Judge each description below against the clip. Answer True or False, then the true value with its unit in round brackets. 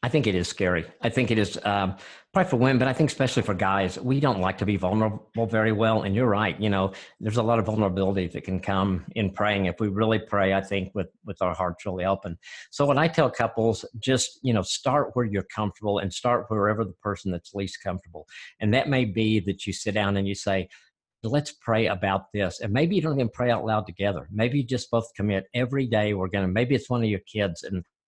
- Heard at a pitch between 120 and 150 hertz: False (105 Hz)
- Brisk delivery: True (245 wpm)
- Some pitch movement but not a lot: True (3.5 semitones)